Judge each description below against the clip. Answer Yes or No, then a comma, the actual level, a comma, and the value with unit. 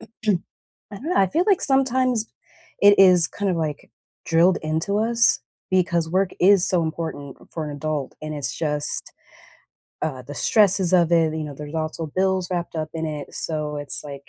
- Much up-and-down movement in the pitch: No, average, 4.0 semitones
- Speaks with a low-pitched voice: No, medium, 165 Hz